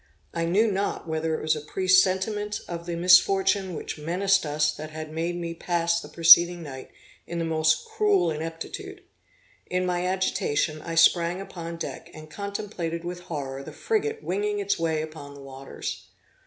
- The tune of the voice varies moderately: Yes, average, 3.2 semitones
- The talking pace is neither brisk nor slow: Yes, average, 170 wpm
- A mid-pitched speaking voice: Yes, medium, 170 Hz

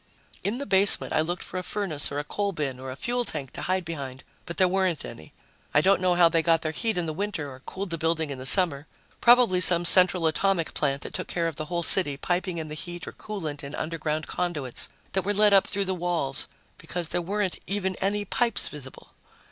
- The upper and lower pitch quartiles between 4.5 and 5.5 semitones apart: No, average, 3.9 semitones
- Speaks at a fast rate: Yes, fast, 235 wpm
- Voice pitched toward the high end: No, medium, 175 Hz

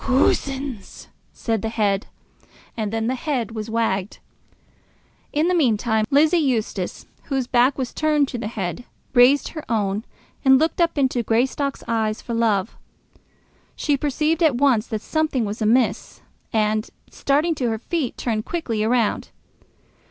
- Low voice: No, high, 240 Hz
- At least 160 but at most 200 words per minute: No, average, 145 wpm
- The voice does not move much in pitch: No, average, 4.4 semitones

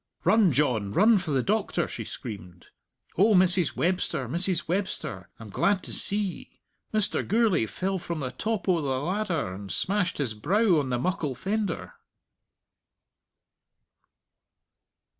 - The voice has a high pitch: No, medium, 175 Hz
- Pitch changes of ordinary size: No, wide, 7.6 semitones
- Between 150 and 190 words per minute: No, average, 140 wpm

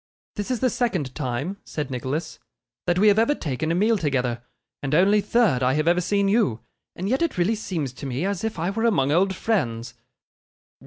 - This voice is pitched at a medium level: Yes, medium, 175 Hz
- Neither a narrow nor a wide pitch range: No, wide, 7.4 semitones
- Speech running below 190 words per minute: No, fast, 205 wpm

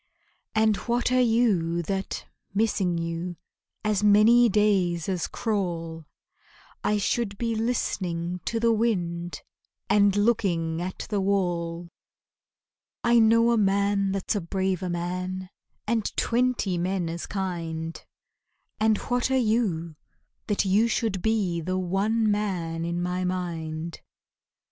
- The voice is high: Yes, high, 195 Hz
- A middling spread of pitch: Yes, average, 4.0 semitones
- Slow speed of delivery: Yes, slow, 125 wpm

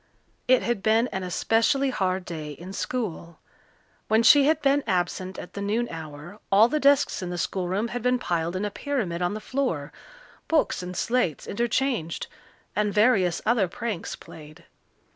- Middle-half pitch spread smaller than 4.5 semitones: No, wide, 5.6 semitones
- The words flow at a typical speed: Yes, average, 165 wpm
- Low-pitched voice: No, high, 205 Hz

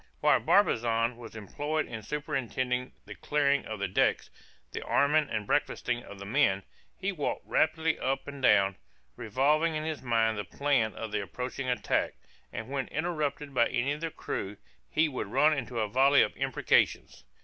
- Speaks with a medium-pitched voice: No, low, 130 Hz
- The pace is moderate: Yes, average, 170 wpm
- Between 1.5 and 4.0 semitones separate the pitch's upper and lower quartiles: No, average, 4.9 semitones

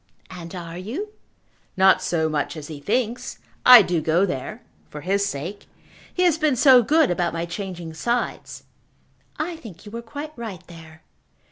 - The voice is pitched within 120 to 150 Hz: No, high, 190 Hz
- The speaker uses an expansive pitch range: Yes, wide, 6.5 semitones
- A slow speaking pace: No, average, 165 wpm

